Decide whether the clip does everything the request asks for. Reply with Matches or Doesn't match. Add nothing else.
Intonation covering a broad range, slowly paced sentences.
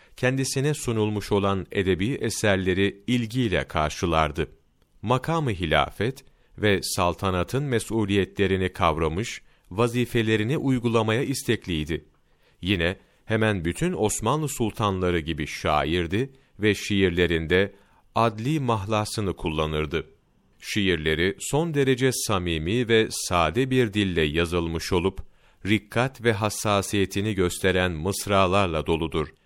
Doesn't match